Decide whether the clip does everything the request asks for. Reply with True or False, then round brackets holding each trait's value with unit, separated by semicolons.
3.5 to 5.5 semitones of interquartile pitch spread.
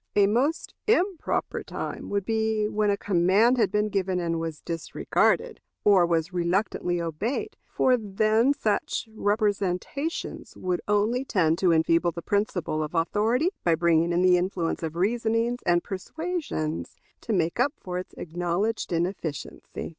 True (4.4 semitones)